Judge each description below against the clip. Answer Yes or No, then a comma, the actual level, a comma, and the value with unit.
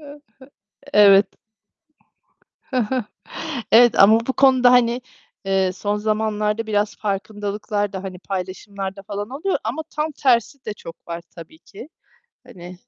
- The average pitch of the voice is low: No, high, 210 Hz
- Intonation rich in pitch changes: No, average, 3.3 semitones